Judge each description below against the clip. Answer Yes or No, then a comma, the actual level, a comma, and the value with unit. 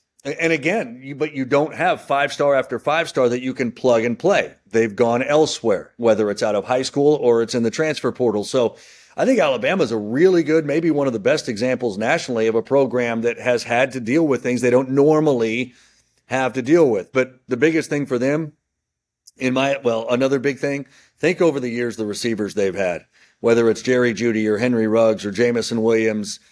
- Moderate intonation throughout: Yes, average, 3.6 semitones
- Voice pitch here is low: Yes, low, 125 Hz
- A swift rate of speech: Yes, fast, 215 wpm